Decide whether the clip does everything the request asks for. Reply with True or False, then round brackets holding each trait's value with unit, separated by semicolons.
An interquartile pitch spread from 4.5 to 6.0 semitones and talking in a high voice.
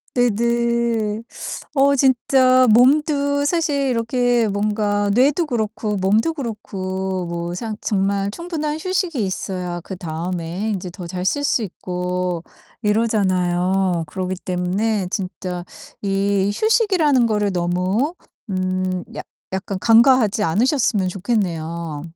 True (5.1 semitones; 205 Hz)